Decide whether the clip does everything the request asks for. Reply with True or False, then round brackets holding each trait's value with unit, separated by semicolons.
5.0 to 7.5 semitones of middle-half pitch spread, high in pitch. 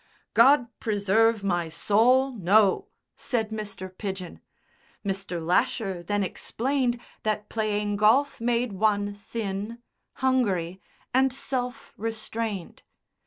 False (3.5 semitones; 215 Hz)